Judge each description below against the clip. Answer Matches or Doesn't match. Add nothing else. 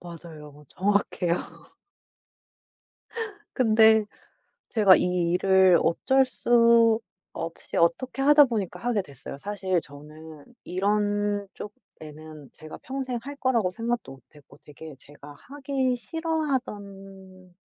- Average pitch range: Doesn't match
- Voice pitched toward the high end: Matches